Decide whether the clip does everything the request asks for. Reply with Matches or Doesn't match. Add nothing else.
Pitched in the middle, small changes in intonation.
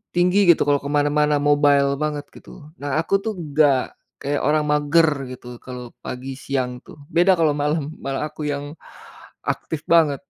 Matches